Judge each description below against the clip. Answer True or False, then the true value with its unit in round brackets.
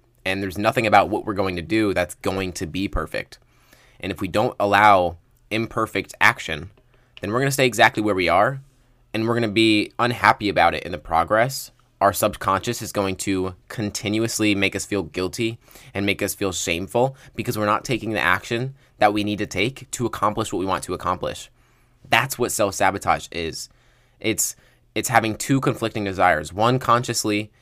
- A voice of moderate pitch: False (110 Hz)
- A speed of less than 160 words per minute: False (185 wpm)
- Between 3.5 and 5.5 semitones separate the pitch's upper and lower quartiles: True (3.8 semitones)